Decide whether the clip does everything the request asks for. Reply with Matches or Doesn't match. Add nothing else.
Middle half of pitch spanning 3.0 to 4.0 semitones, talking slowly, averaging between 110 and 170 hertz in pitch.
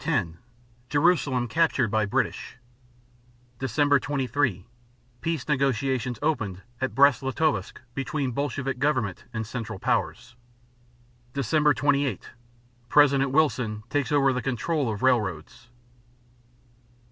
Matches